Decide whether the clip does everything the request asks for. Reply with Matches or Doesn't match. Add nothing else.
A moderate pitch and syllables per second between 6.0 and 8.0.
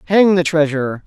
Doesn't match